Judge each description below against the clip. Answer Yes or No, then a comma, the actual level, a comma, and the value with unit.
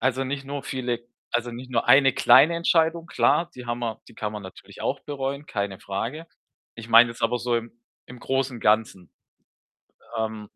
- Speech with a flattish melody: No, average, 3.2 semitones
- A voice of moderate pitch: No, low, 120 Hz